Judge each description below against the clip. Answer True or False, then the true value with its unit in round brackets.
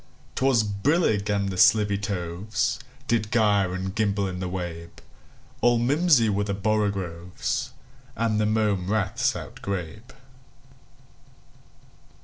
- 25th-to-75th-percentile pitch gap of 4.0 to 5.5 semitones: False (2.6 semitones)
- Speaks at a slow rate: True (105 wpm)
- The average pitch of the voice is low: True (100 Hz)